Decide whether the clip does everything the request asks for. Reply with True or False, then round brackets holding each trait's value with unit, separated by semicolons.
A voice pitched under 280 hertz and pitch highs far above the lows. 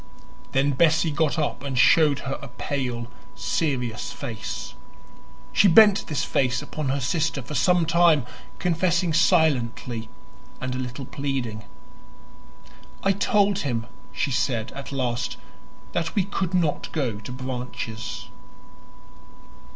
False (140 Hz; 5.0 semitones)